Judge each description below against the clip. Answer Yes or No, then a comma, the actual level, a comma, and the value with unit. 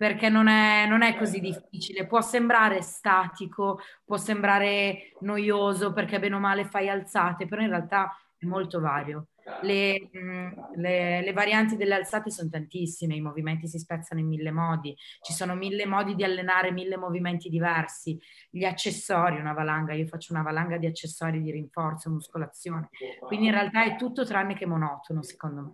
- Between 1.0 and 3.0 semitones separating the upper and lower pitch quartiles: No, average, 3.5 semitones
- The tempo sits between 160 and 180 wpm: Yes, fast, 170 wpm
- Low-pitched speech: No, medium, 185 Hz